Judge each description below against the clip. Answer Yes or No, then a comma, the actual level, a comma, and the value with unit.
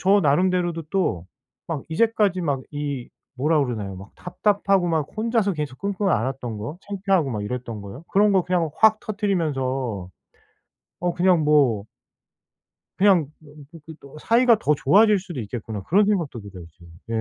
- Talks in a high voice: No, medium, 160 Hz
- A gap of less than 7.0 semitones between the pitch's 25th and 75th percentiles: No, wide, 7.4 semitones